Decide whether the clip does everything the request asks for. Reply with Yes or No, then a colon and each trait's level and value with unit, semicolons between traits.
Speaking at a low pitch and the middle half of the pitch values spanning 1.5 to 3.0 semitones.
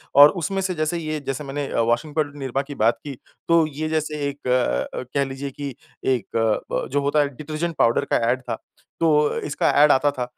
No: medium, 145 Hz; average, 2.7 semitones